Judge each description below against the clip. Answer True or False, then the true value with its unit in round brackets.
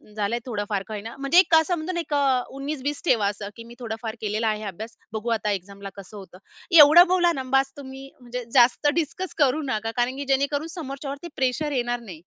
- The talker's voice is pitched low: False (255 Hz)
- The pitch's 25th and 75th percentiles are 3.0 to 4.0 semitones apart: False (4.9 semitones)